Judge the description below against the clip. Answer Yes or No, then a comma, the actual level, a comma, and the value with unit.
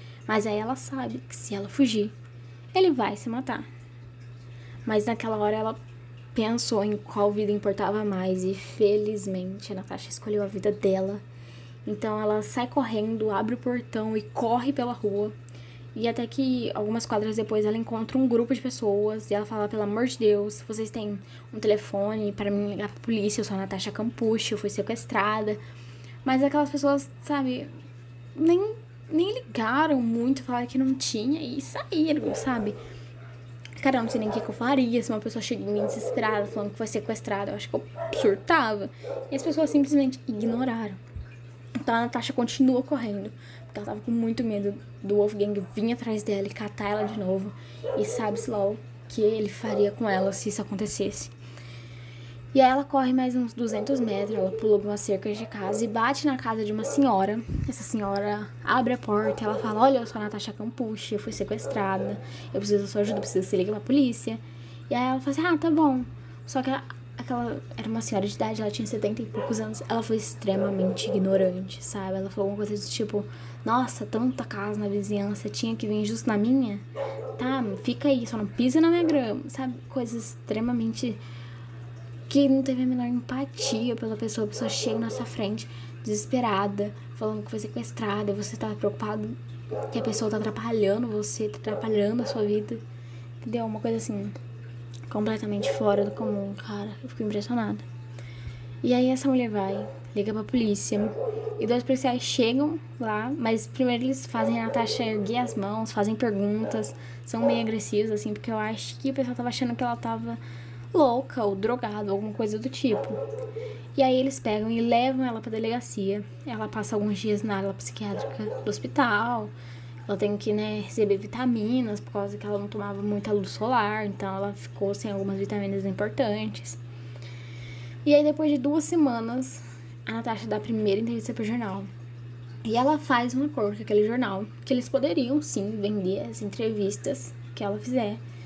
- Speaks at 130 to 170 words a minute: No, fast, 185 wpm